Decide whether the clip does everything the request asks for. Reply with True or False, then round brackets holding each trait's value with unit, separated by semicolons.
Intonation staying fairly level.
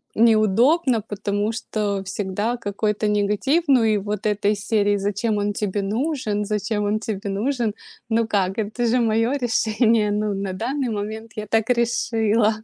True (2.0 semitones)